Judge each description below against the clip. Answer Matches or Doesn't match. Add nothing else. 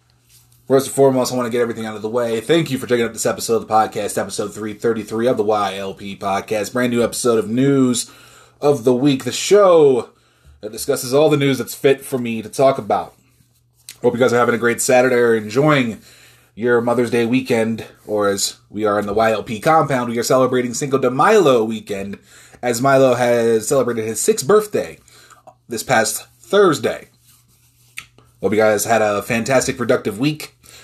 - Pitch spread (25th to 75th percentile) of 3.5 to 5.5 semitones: Doesn't match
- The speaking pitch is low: Matches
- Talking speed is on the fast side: Doesn't match